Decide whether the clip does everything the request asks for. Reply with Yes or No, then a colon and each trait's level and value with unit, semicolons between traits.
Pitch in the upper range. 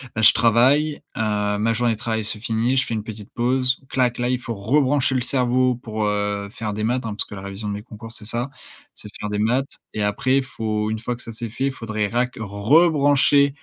No: low, 115 Hz